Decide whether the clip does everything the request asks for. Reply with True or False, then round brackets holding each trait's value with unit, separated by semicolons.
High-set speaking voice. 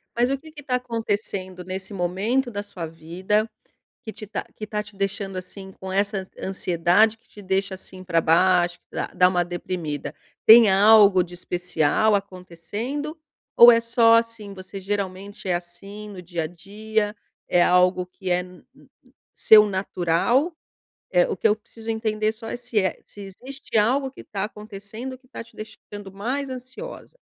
True (205 Hz)